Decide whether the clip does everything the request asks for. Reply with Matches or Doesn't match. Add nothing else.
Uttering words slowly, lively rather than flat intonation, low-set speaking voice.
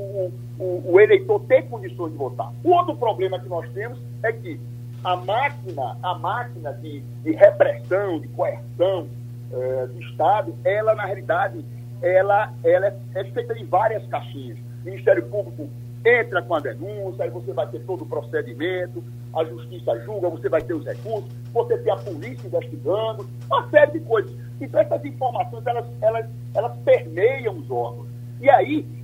Doesn't match